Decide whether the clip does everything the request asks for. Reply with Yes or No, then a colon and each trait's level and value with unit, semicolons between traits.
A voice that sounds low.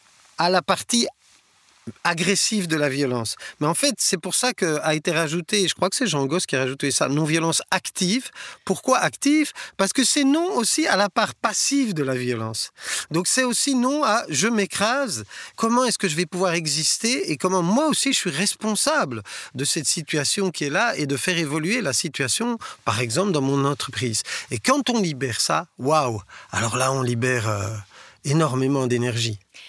No: medium, 170 Hz